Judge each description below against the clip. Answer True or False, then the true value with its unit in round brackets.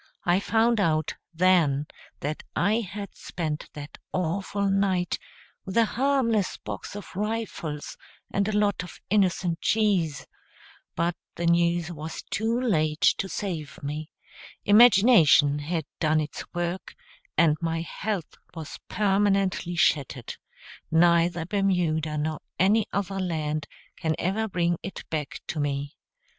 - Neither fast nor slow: False (125 wpm)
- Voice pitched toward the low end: False (175 Hz)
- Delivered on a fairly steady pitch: False (4.3 semitones)